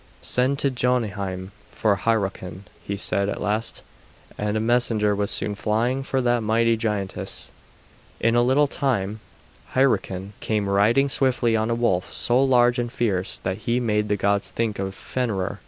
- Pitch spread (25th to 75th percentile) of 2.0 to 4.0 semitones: Yes, average, 3.2 semitones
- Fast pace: No, average, 160 wpm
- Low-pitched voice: Yes, low, 110 Hz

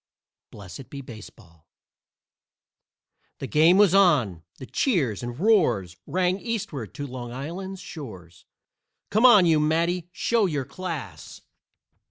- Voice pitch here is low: No, medium, 150 Hz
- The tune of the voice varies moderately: No, wide, 7.5 semitones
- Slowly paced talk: Yes, slow, 120 wpm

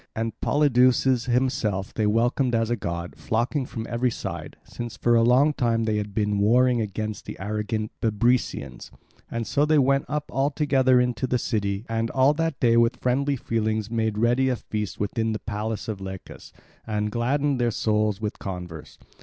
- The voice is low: Yes, low, 115 Hz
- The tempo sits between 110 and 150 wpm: No, average, 180 wpm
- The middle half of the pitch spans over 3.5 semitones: No, average, 3.2 semitones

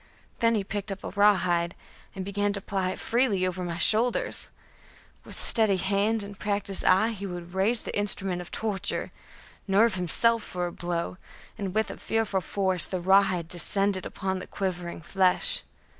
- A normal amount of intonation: No, narrow, 2.3 semitones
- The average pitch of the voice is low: No, high, 195 Hz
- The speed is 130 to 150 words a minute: No, average, 165 wpm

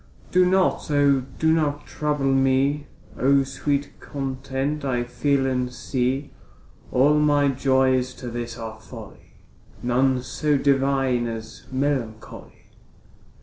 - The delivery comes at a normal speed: No, slow, 115 wpm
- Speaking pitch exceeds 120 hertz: Yes, low, 135 Hz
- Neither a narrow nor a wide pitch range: No, narrow, 2.2 semitones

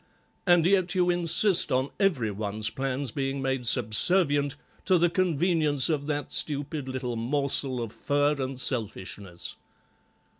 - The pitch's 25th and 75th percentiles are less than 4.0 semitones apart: No, average, 4.8 semitones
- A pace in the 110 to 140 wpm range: Yes, slow, 135 wpm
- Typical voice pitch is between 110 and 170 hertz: Yes, medium, 140 Hz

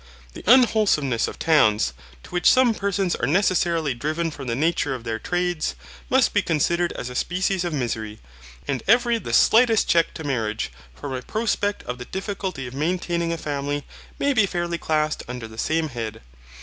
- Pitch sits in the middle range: Yes, medium, 160 Hz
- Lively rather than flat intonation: Yes, wide, 6.7 semitones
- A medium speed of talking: Yes, average, 180 wpm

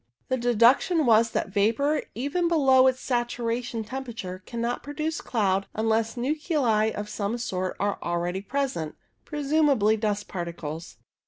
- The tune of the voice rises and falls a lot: No, average, 4.7 semitones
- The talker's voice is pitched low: No, high, 235 Hz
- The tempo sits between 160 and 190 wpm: No, average, 145 wpm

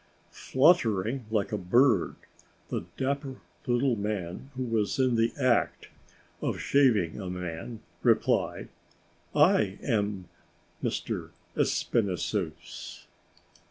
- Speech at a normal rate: No, slow, 95 wpm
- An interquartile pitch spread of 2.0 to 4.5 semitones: No, average, 5.0 semitones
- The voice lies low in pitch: Yes, low, 110 Hz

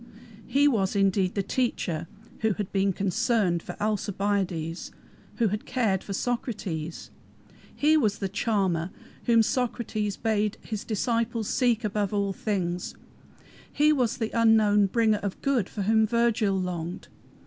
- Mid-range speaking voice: No, high, 210 Hz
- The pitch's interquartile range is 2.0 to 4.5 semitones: Yes, average, 3.1 semitones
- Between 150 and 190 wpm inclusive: No, slow, 135 wpm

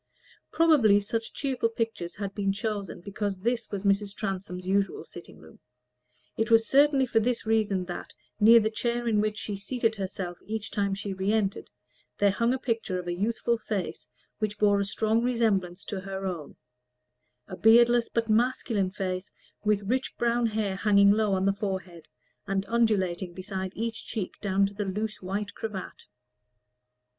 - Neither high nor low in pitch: No, high, 205 Hz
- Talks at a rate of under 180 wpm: Yes, average, 170 wpm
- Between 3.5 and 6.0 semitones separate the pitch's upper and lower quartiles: No, narrow, 2.6 semitones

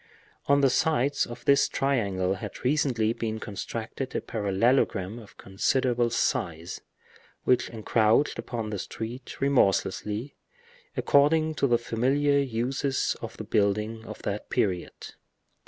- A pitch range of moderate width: Yes, average, 4.3 semitones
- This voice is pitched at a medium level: No, low, 115 Hz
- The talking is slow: Yes, slow, 120 wpm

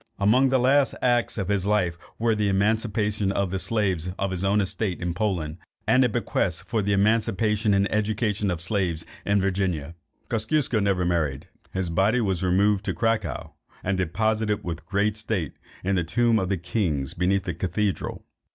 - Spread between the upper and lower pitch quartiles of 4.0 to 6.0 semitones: No, average, 3.1 semitones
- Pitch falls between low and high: No, low, 100 Hz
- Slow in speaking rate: No, average, 180 wpm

